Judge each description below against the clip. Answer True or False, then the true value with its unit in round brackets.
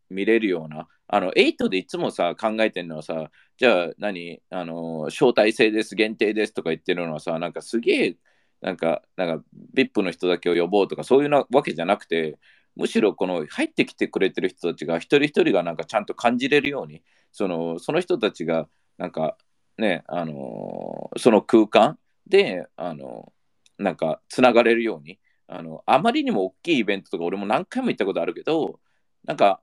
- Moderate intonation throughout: False (7.2 semitones)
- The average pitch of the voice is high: False (105 Hz)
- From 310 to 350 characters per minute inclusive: False (360 characters per minute)